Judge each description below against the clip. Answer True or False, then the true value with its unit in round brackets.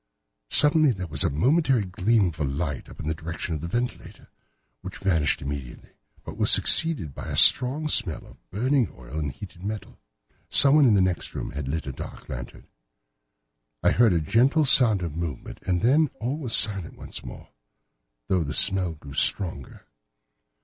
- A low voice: True (95 Hz)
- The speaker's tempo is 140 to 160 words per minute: False (175 wpm)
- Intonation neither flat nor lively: False (8.0 semitones)